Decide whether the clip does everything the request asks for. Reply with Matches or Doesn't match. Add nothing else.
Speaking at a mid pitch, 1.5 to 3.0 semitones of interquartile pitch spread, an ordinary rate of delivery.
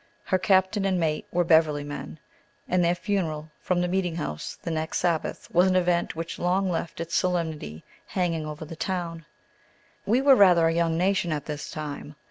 Matches